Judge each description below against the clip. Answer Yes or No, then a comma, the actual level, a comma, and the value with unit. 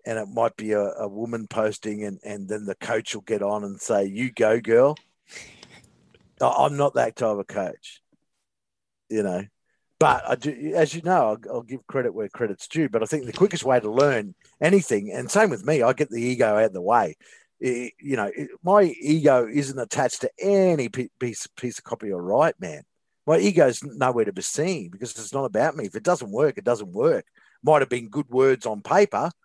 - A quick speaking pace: Yes, fast, 215 wpm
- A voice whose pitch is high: No, low, 125 Hz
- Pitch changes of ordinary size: No, wide, 6.0 semitones